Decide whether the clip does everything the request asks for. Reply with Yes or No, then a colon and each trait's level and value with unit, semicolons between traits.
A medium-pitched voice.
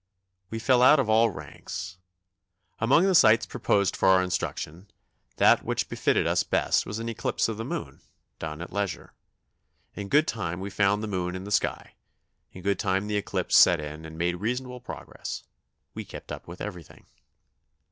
No: low, 100 Hz